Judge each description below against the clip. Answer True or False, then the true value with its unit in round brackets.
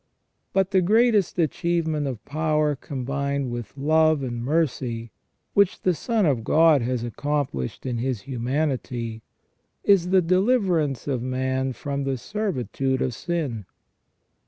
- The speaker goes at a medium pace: False (130 wpm)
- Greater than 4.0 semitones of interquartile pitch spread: True (4.9 semitones)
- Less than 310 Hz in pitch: True (140 Hz)